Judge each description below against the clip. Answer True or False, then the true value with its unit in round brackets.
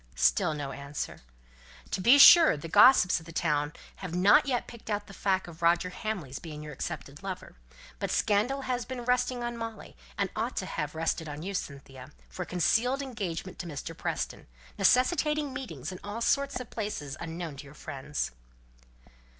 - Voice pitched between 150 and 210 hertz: True (185 Hz)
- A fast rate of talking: False (175 wpm)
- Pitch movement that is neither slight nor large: False (7.8 semitones)